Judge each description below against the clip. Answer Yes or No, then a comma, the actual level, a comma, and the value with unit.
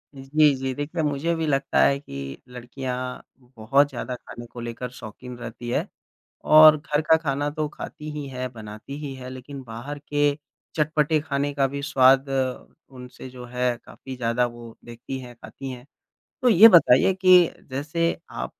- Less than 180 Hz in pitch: Yes, low, 135 Hz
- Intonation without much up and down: No, average, 3.0 semitones